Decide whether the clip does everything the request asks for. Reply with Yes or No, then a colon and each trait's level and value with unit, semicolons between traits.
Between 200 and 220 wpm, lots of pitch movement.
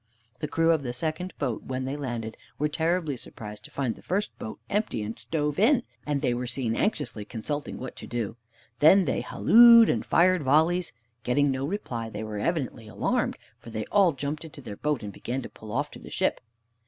Yes: fast, 205 wpm; wide, 5.9 semitones